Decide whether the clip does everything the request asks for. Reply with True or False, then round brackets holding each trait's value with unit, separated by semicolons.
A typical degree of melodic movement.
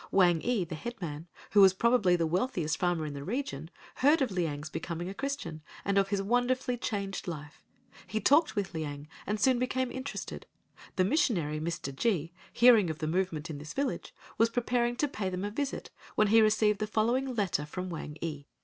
False (6.8 semitones)